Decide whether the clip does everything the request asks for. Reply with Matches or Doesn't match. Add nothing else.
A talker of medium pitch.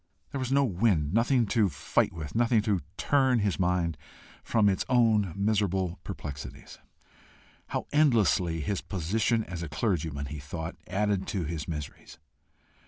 Doesn't match